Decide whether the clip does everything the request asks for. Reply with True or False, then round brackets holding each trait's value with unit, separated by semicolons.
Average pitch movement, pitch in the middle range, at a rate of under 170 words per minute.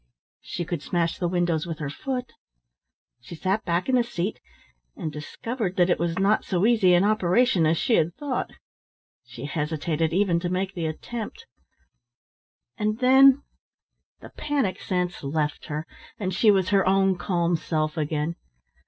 True (4.5 semitones; 180 Hz; 160 wpm)